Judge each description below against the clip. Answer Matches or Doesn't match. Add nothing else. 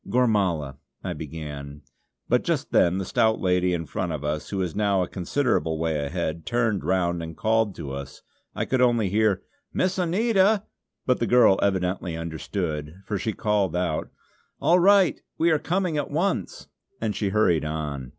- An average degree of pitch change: Doesn't match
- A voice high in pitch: Doesn't match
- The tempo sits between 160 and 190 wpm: Matches